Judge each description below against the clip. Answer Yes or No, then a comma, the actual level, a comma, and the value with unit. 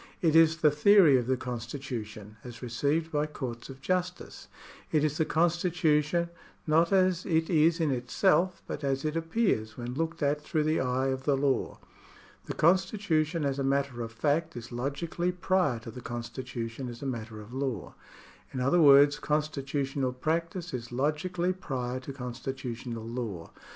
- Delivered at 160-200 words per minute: Yes, average, 170 wpm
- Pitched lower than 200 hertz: Yes, medium, 140 Hz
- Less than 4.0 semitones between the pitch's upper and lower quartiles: No, average, 4.7 semitones